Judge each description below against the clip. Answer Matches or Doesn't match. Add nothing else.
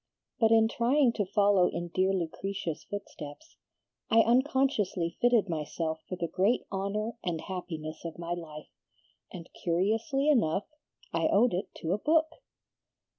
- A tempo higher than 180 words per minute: Doesn't match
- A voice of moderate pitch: Doesn't match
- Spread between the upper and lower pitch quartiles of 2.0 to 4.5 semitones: Doesn't match